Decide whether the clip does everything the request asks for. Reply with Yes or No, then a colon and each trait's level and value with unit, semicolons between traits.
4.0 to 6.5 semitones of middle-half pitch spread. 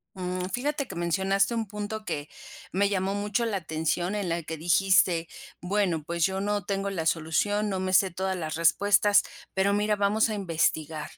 No: average, 3.2 semitones